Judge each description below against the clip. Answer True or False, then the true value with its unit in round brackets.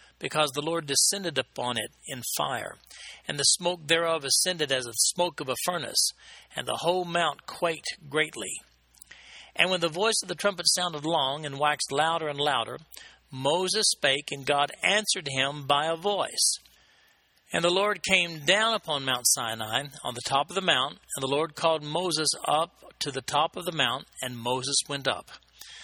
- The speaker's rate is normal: True (180 wpm)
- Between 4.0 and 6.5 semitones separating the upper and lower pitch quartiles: True (4.3 semitones)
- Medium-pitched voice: True (155 Hz)